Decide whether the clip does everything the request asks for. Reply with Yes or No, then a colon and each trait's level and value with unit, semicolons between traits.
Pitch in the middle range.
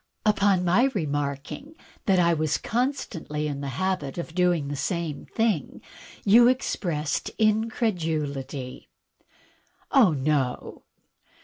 Yes: medium, 170 Hz